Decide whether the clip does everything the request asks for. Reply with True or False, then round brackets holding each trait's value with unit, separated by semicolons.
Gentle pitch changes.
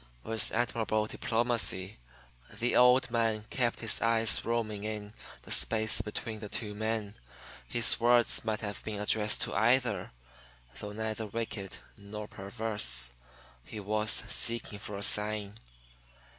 True (1.8 semitones)